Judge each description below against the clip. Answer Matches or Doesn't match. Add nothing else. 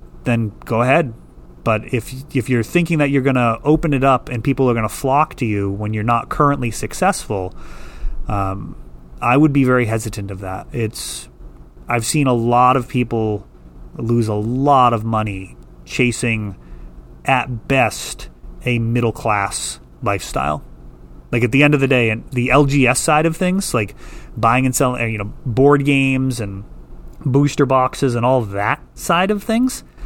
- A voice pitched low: Matches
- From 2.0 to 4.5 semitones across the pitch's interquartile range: Doesn't match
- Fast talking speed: Doesn't match